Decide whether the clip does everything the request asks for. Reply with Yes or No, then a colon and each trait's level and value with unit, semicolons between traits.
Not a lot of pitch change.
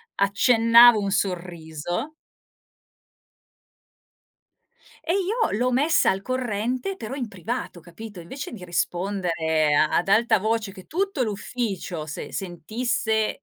No: wide, 5.7 semitones